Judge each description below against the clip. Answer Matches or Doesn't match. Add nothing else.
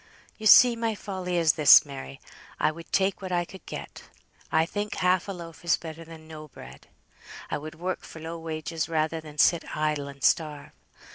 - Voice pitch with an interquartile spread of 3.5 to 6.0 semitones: Doesn't match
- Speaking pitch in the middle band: Matches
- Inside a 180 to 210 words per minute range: Matches